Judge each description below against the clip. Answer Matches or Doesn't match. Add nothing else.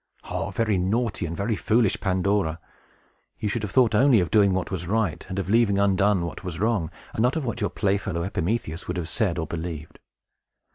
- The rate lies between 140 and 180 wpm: Doesn't match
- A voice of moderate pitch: Doesn't match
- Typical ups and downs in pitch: Matches